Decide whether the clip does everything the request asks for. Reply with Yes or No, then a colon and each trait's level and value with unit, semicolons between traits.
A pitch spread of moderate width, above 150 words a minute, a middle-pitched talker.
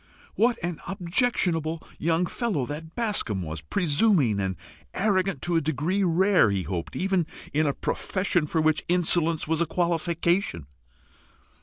No: average, 4.0 semitones; average, 140 wpm; medium, 165 Hz